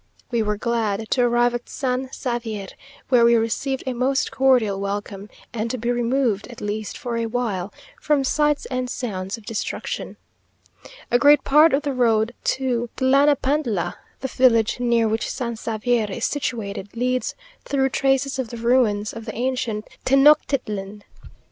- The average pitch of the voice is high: Yes, high, 240 Hz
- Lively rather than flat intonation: No, average, 3.2 semitones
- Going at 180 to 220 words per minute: No, average, 155 wpm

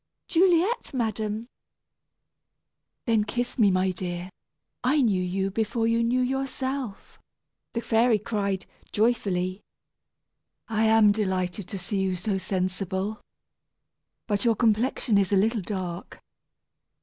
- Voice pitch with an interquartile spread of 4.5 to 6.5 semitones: No, average, 3.6 semitones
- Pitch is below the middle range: No, high, 210 Hz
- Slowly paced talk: Yes, slow, 115 wpm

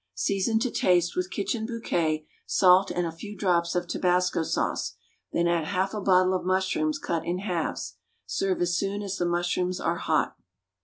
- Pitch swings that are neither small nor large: No, narrow, 2.2 semitones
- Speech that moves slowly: No, average, 175 wpm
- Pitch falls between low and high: Yes, medium, 180 Hz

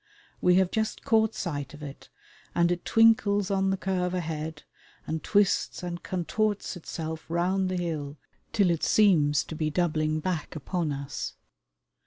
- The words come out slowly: No, average, 155 wpm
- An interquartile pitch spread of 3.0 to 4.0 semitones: Yes, average, 3.7 semitones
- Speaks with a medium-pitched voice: Yes, medium, 175 Hz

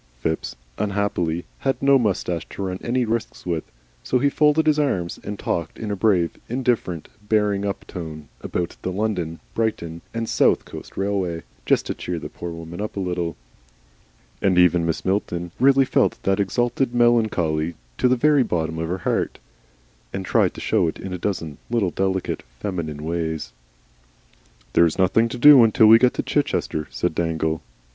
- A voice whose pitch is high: No, very low, 95 Hz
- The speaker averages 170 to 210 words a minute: Yes, average, 175 wpm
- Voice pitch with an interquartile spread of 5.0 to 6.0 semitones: Yes, average, 5.3 semitones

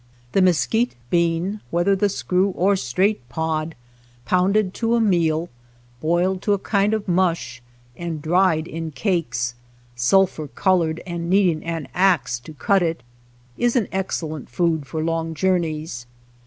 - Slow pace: No, average, 145 wpm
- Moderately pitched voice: Yes, medium, 170 Hz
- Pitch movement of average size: Yes, average, 3.3 semitones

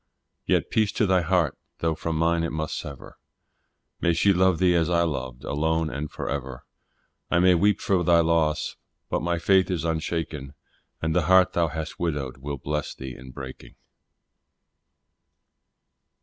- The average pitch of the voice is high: No, very low, 80 Hz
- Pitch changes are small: No, average, 3.0 semitones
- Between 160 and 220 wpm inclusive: Yes, average, 165 wpm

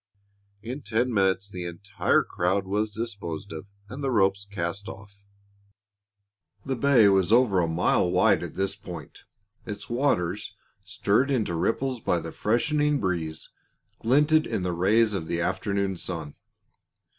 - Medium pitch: No, low, 100 Hz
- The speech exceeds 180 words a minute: No, average, 145 wpm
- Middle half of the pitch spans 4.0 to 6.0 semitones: Yes, average, 4.4 semitones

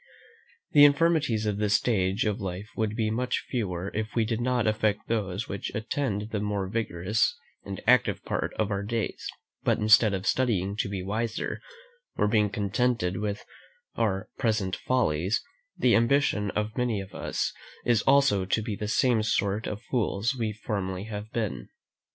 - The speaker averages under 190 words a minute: Yes, average, 165 wpm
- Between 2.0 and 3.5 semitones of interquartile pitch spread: Yes, narrow, 2.6 semitones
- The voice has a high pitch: No, low, 105 Hz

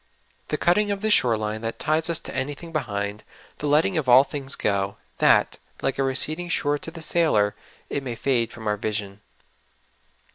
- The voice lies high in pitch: No, low, 135 Hz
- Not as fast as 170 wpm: No, average, 185 wpm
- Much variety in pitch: Yes, wide, 6.5 semitones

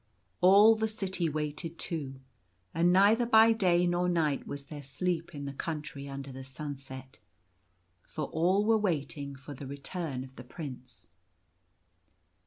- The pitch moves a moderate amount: Yes, average, 4.7 semitones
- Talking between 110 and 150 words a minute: Yes, average, 145 wpm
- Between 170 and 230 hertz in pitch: No, medium, 155 Hz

